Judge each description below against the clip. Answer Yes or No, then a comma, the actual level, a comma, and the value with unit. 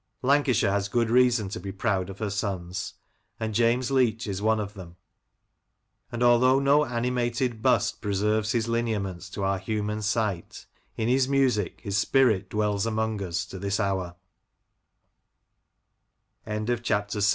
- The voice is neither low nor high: No, low, 110 Hz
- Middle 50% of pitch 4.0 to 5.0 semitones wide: No, average, 3.2 semitones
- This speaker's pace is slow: Yes, slow, 125 wpm